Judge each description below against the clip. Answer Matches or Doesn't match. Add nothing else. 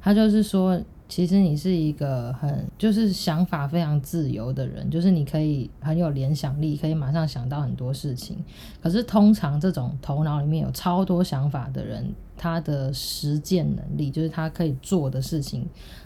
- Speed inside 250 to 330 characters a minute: Matches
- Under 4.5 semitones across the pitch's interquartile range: Matches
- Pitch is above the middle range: Doesn't match